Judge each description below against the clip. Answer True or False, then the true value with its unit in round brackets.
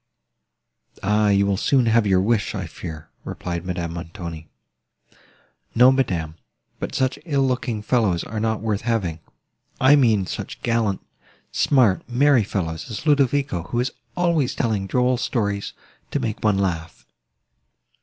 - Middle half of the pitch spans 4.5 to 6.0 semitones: True (5.2 semitones)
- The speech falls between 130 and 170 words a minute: True (140 wpm)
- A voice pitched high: False (105 Hz)